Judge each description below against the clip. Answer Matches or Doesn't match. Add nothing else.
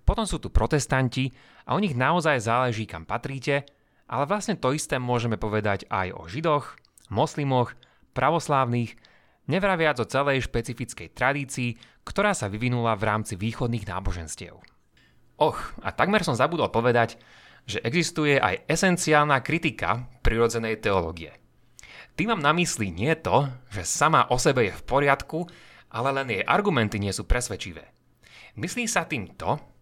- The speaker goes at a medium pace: Matches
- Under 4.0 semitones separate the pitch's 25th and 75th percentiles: Doesn't match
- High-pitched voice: Doesn't match